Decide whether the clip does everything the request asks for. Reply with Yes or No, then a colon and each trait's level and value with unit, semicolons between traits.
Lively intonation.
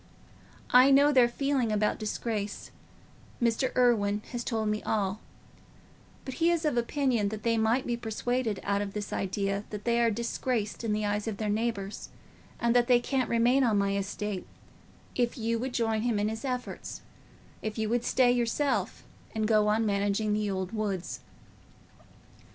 No: average, 2.7 semitones